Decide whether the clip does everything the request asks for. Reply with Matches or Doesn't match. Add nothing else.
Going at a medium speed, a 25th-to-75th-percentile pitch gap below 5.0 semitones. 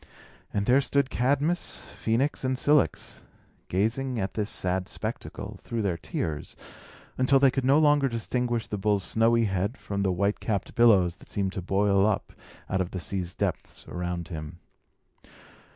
Doesn't match